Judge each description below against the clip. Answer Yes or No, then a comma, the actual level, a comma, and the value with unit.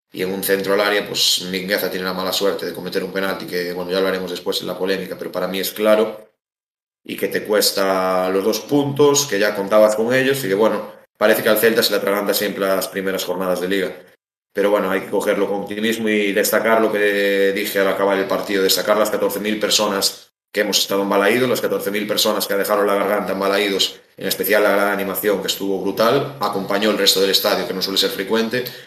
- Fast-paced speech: Yes, fast, 230 wpm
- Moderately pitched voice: No, low, 100 Hz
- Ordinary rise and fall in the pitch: No, narrow, 1.7 semitones